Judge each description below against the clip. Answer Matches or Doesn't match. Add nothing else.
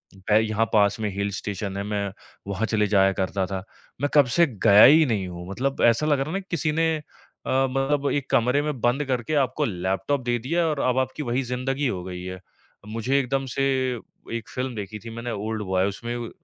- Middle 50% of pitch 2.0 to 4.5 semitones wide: Doesn't match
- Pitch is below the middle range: Matches